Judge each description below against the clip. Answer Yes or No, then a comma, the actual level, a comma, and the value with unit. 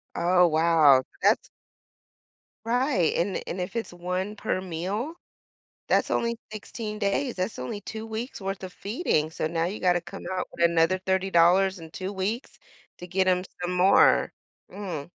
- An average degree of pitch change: Yes, average, 3.2 semitones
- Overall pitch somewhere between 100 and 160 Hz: No, medium, 185 Hz